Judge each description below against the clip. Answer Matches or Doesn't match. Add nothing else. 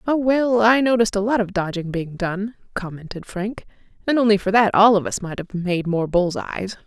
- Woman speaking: Matches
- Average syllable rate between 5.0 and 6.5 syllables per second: Matches